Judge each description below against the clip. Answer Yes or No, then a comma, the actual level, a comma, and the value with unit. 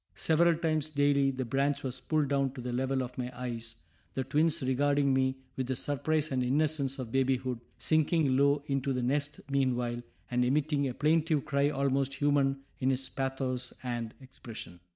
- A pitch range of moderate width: No, narrow, 2.1 semitones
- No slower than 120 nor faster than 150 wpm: No, average, 170 wpm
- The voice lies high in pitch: No, low, 135 Hz